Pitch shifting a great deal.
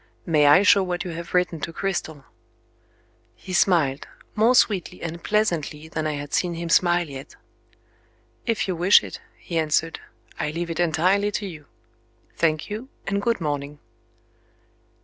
No: average, 3.7 semitones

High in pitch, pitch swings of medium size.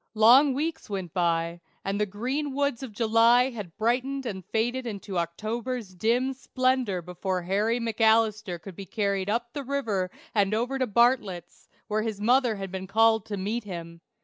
Yes: high, 220 Hz; average, 4.1 semitones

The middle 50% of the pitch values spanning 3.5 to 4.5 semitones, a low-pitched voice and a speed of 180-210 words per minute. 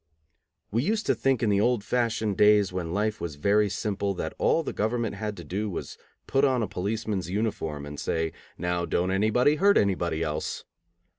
Yes: average, 4.0 semitones; low, 105 Hz; average, 195 wpm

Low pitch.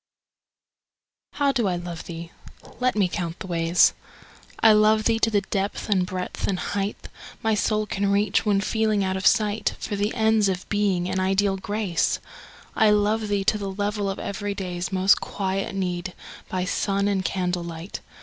No: high, 200 Hz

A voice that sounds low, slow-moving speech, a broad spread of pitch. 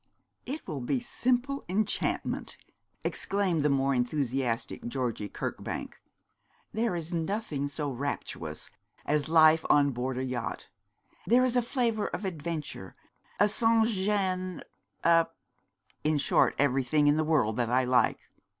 No: medium, 155 Hz; slow, 130 wpm; wide, 7.3 semitones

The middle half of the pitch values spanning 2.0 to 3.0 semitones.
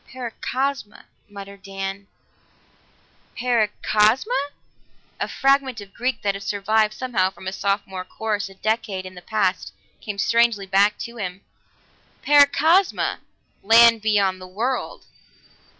No: average, 3.4 semitones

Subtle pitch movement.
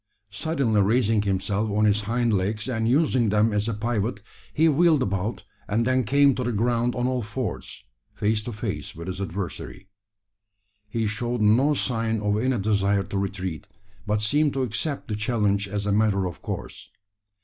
No: average, 3.2 semitones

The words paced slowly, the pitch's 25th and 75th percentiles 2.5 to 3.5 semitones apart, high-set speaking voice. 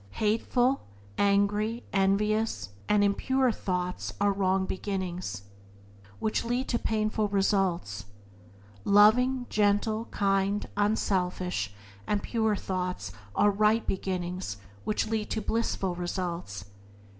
Yes: slow, 105 wpm; average, 2.9 semitones; high, 200 Hz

